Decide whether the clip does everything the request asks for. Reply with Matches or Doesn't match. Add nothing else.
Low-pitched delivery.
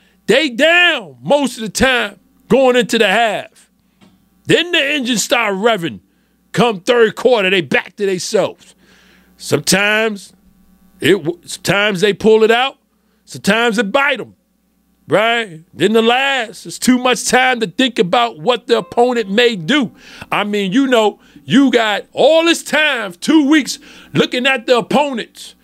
Doesn't match